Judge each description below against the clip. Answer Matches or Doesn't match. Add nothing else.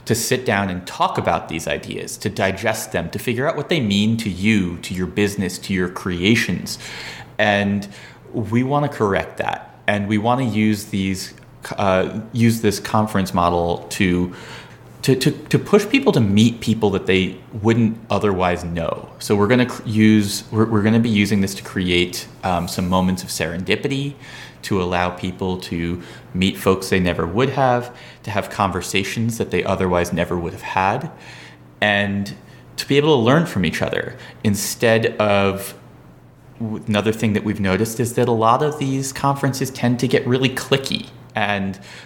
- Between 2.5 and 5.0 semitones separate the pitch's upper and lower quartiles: Matches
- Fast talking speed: Doesn't match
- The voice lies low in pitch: Matches